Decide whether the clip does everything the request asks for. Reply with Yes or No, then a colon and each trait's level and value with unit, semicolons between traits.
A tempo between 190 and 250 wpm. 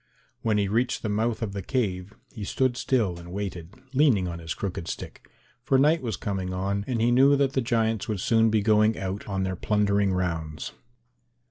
Yes: average, 200 wpm